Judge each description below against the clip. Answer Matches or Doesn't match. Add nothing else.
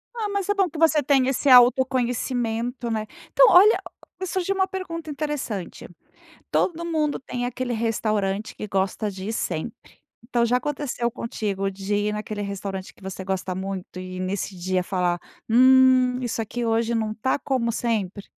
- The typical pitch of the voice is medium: Doesn't match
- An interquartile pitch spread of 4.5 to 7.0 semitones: Matches